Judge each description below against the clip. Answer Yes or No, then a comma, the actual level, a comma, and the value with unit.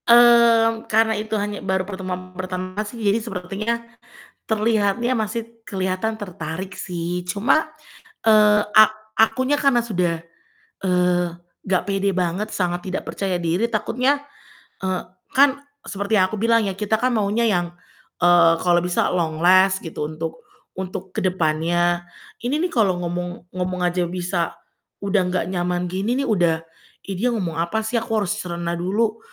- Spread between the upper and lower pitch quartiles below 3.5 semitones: No, average, 3.8 semitones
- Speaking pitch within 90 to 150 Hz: No, high, 190 Hz